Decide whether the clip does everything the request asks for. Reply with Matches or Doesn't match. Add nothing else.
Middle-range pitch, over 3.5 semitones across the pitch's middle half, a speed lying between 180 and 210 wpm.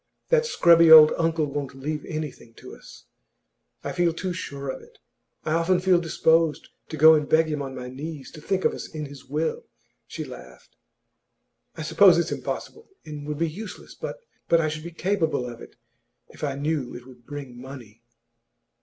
Doesn't match